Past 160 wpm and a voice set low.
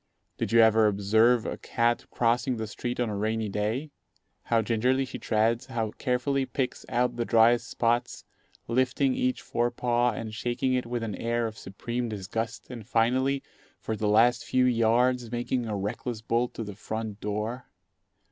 Yes: average, 170 wpm; low, 115 Hz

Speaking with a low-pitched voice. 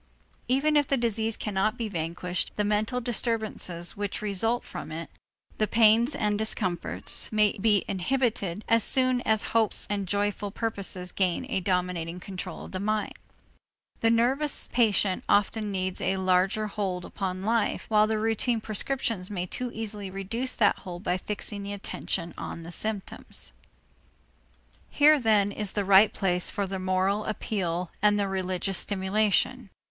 No: high, 205 Hz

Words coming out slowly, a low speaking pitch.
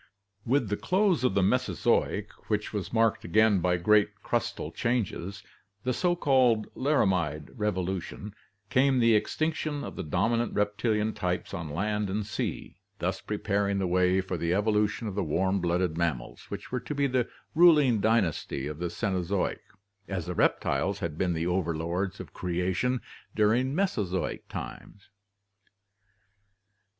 No: average, 150 wpm; low, 105 Hz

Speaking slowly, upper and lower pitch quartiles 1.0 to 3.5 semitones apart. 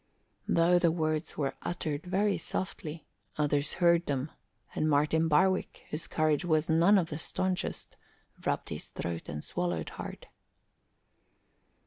Yes: slow, 130 wpm; average, 2.9 semitones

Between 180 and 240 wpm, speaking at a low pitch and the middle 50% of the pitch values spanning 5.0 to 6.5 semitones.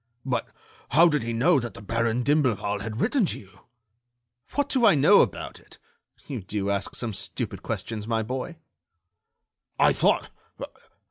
No: average, 155 wpm; low, 115 Hz; wide, 5.5 semitones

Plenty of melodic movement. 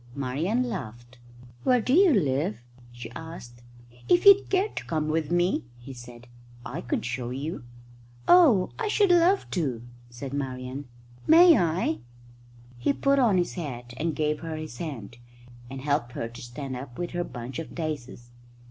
Yes: wide, 7.3 semitones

